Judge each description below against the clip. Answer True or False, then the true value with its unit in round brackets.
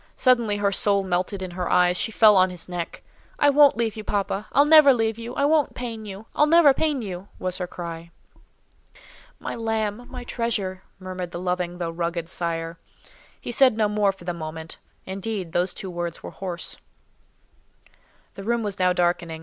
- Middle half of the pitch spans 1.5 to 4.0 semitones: False (4.4 semitones)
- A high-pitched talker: True (195 Hz)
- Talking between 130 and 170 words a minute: False (180 wpm)